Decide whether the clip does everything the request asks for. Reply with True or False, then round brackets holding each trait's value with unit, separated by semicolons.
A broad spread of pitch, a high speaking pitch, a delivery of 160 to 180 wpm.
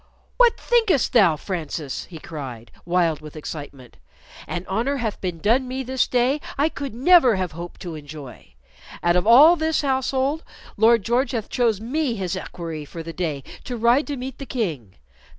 True (8.2 semitones; 220 Hz; 175 wpm)